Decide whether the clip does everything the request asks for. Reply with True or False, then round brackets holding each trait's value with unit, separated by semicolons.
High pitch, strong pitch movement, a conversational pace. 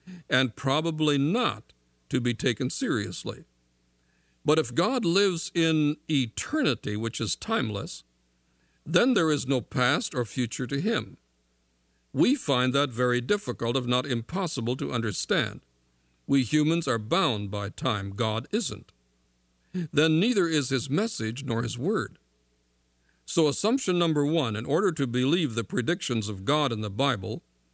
False (125 Hz; 9.0 semitones; 145 wpm)